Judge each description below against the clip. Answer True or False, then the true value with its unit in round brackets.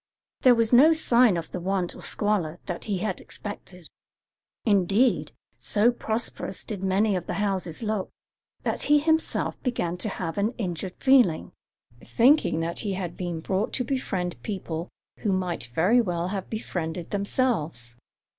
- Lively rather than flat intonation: False (4.6 semitones)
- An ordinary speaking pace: True (155 wpm)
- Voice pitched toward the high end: True (195 Hz)